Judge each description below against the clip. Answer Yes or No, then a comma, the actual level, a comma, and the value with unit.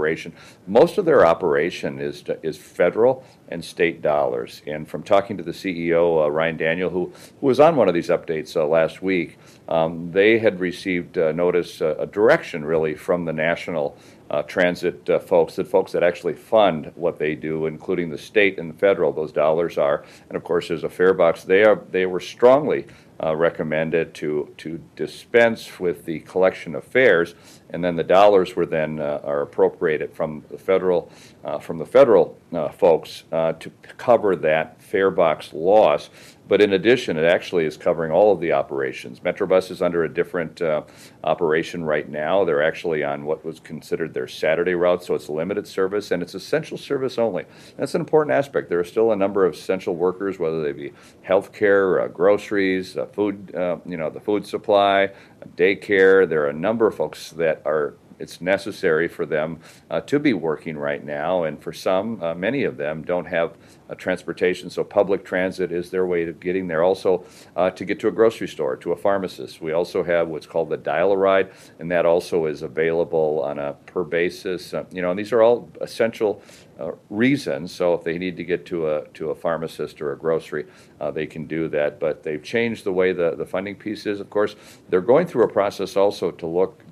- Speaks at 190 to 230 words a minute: Yes, average, 200 wpm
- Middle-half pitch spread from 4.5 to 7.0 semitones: Yes, average, 5.0 semitones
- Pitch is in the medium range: No, very low, 90 Hz